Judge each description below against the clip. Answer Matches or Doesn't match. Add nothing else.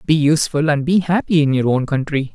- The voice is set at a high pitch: Doesn't match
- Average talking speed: Doesn't match